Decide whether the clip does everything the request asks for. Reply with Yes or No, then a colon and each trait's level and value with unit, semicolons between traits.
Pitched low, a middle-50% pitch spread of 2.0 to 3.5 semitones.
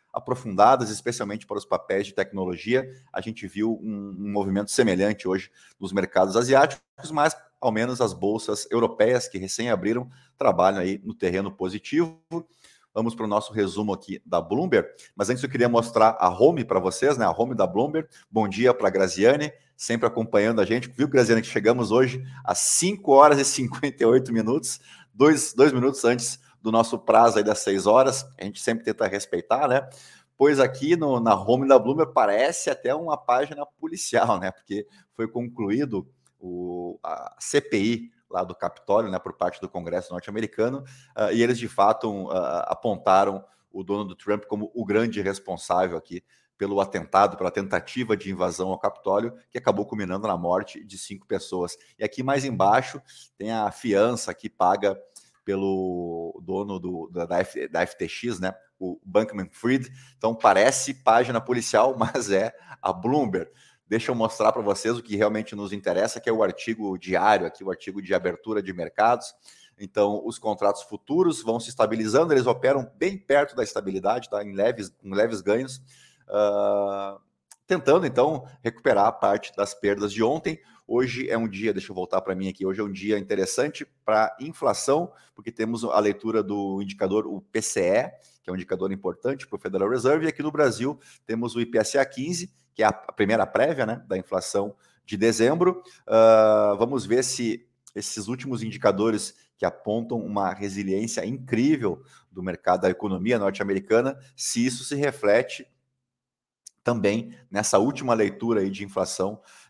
No: low, 110 Hz; average, 4.3 semitones